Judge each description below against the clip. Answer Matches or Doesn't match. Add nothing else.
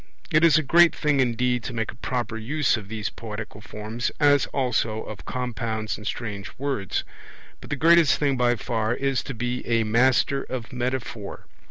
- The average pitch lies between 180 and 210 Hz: Doesn't match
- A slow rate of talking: Doesn't match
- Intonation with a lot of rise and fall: Doesn't match